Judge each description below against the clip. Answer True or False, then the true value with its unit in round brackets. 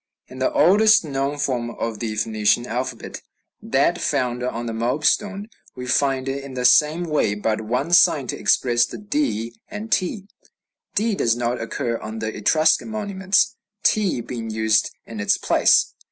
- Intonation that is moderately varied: False (7.2 semitones)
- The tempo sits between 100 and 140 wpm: False (165 wpm)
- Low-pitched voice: True (130 Hz)